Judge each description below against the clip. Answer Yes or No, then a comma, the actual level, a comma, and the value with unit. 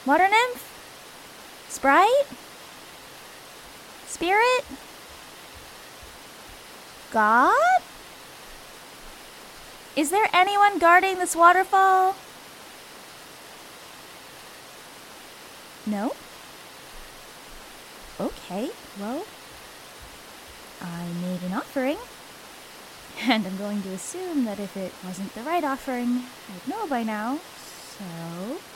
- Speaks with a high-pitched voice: Yes, very high, 275 Hz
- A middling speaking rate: No, slow, 75 wpm